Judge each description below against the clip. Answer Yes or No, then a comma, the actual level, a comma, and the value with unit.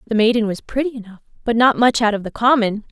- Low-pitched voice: No, high, 225 Hz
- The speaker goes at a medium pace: No, fast, 245 wpm